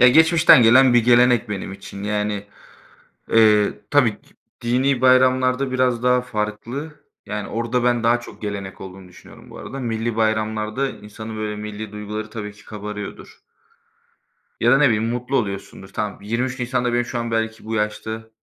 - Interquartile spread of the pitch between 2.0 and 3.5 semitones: Yes, average, 2.9 semitones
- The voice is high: No, low, 115 Hz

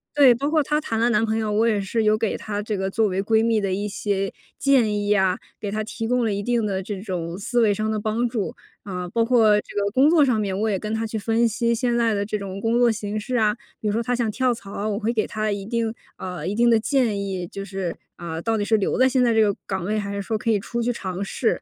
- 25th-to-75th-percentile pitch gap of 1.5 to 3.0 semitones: Yes, narrow, 2.6 semitones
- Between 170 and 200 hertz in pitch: No, high, 215 Hz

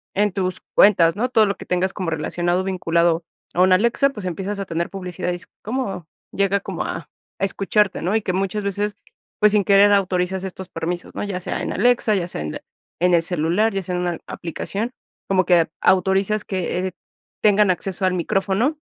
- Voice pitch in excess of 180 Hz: Yes, high, 190 Hz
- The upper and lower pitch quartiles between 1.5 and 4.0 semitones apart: Yes, narrow, 2.4 semitones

